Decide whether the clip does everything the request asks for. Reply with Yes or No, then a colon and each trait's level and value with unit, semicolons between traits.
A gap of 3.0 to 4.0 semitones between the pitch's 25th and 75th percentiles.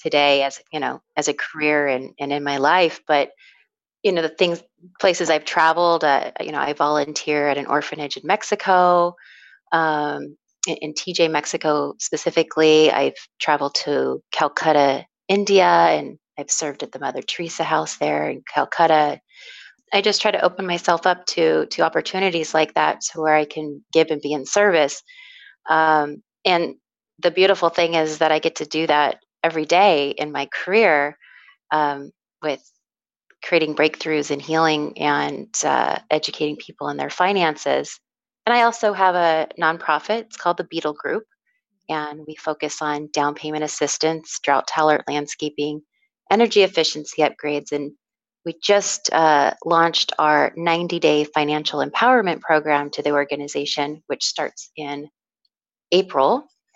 Yes: average, 3.3 semitones